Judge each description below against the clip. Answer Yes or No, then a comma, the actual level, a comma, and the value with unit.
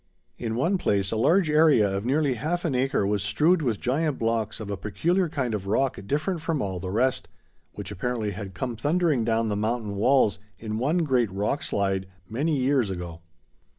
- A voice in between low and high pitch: No, low, 120 Hz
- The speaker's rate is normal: Yes, average, 190 wpm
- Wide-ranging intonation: Yes, wide, 6.3 semitones